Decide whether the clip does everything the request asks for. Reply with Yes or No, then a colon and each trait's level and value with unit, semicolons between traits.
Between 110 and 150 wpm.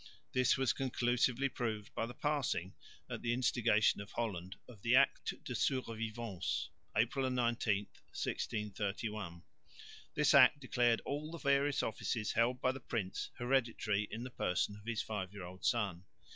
Yes: average, 145 wpm